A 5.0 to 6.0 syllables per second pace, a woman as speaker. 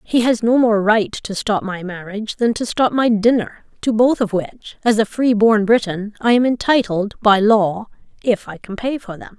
No: 4.8 syllables/s; female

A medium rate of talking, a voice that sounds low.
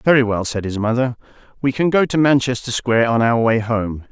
No: fast, 220 wpm; low, 120 Hz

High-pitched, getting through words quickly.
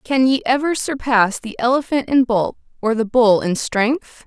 No: high, 245 Hz; average, 185 wpm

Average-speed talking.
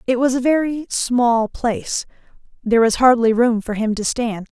Yes: average, 185 wpm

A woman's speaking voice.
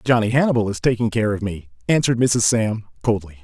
No: male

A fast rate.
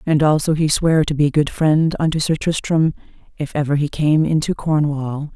No: average, 190 wpm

